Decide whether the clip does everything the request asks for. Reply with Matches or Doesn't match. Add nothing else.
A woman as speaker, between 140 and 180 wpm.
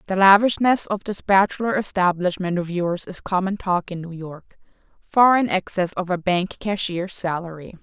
Matches